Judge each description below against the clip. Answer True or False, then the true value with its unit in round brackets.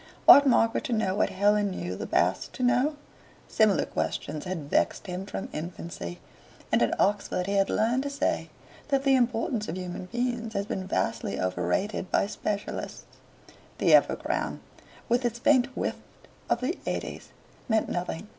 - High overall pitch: True (205 Hz)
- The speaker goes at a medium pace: True (160 wpm)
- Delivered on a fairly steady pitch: False (5.0 semitones)